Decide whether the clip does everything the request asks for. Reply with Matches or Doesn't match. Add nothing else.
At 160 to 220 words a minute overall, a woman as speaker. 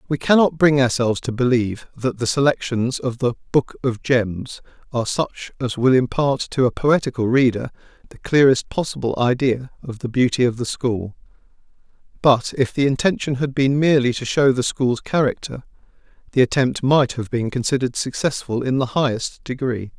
Doesn't match